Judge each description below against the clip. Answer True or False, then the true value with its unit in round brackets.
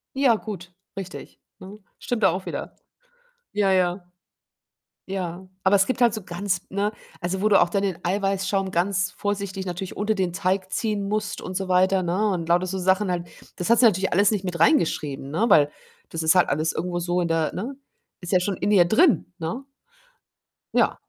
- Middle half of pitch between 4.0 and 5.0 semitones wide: False (2.5 semitones)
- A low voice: False (190 Hz)